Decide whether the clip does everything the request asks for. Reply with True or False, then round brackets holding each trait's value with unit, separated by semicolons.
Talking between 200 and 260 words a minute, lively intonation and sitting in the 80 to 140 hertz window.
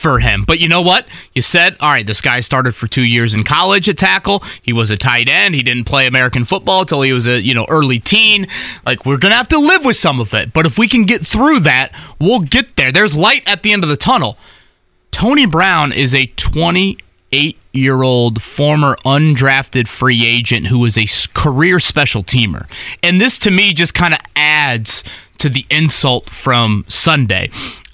True (205 wpm; 6.5 semitones; 135 Hz)